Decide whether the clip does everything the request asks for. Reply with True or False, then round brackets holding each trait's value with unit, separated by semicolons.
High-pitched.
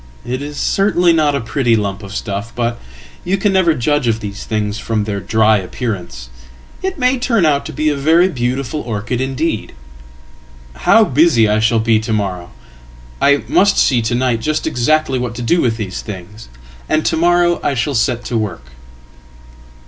False (120 Hz)